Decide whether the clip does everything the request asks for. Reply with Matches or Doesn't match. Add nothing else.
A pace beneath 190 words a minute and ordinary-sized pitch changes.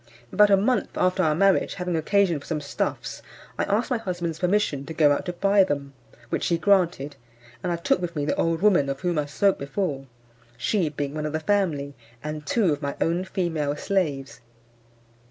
Doesn't match